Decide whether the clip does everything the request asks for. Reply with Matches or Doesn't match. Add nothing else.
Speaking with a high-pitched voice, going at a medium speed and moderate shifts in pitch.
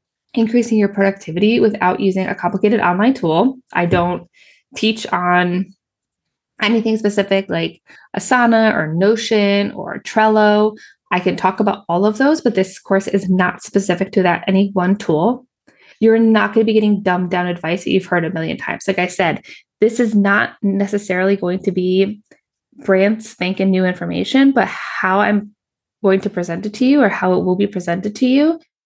Matches